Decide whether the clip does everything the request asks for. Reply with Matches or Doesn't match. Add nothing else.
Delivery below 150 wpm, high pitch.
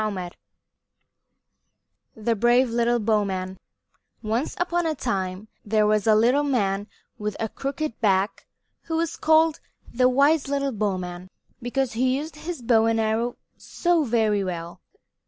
Matches